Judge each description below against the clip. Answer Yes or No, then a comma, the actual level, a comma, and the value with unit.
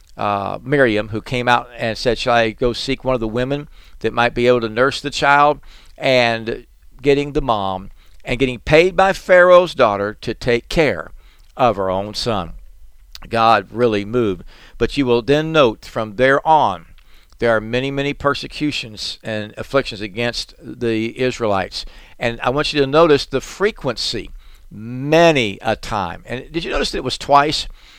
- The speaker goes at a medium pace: Yes, average, 170 wpm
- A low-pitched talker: Yes, low, 120 Hz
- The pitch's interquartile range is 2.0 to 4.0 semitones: No, average, 4.6 semitones